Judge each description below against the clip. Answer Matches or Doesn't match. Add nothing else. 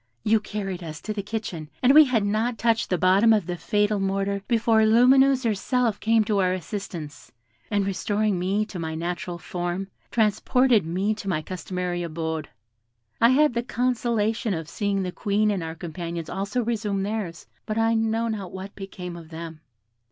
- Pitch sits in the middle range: Doesn't match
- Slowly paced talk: Doesn't match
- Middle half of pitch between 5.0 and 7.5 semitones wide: Doesn't match